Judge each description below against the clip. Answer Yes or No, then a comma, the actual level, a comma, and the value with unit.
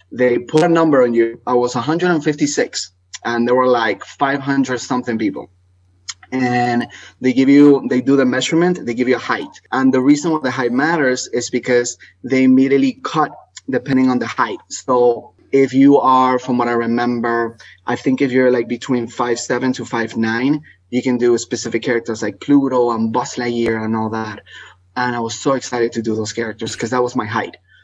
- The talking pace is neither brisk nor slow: Yes, average, 195 wpm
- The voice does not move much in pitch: Yes, narrow, 2.0 semitones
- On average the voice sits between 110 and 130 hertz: Yes, low, 125 Hz